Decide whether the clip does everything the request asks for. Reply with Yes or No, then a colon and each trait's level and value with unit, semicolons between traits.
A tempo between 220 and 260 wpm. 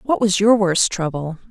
No: average, 200 wpm